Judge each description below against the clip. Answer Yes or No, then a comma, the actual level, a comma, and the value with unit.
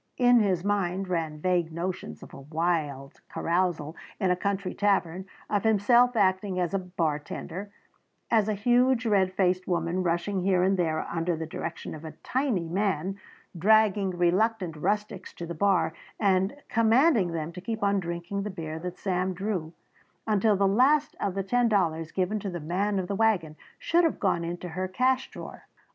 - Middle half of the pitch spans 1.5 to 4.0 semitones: Yes, average, 3.4 semitones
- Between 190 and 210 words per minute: No, average, 175 wpm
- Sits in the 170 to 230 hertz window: Yes, medium, 185 Hz